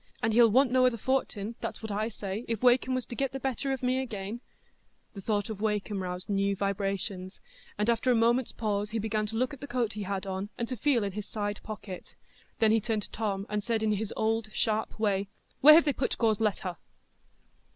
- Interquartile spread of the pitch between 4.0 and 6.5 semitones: No, average, 3.1 semitones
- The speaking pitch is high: Yes, high, 220 Hz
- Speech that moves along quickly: Yes, fast, 225 wpm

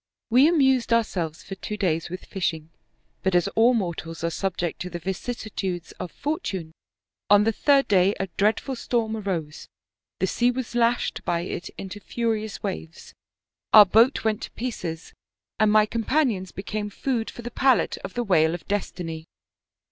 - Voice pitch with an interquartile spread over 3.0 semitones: Yes, average, 4.8 semitones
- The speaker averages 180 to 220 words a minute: No, average, 165 wpm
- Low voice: No, high, 205 Hz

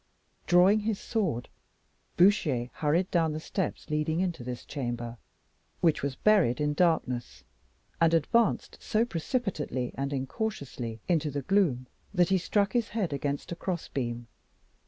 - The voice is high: No, medium, 160 Hz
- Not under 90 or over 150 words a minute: Yes, slow, 135 wpm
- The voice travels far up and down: Yes, wide, 6.4 semitones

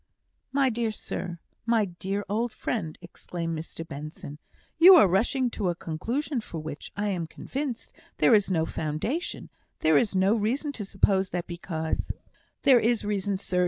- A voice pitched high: Yes, high, 195 Hz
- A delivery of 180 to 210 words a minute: No, average, 165 wpm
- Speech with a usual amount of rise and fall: No, wide, 5.7 semitones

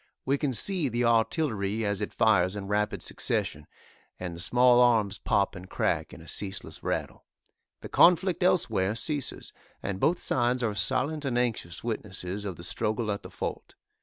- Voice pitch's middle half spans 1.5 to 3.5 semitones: No, average, 4.3 semitones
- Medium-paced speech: Yes, average, 170 wpm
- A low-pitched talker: Yes, low, 110 Hz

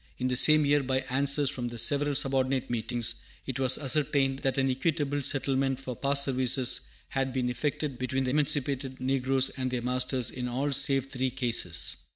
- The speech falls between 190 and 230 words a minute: No, average, 180 wpm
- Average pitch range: No, narrow, 1.6 semitones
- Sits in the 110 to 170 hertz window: Yes, low, 135 Hz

